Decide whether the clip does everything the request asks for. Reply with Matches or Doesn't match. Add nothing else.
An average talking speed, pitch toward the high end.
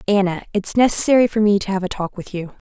Doesn't match